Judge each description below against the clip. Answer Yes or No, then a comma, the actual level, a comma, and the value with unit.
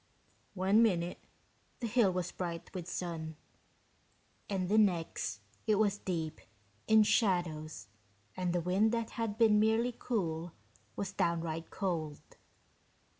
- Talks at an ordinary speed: No, slow, 125 wpm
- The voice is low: No, medium, 185 Hz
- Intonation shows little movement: No, average, 4.2 semitones